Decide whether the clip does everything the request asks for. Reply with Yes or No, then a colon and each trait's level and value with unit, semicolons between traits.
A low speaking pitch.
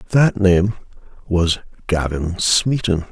Yes: very low, 95 Hz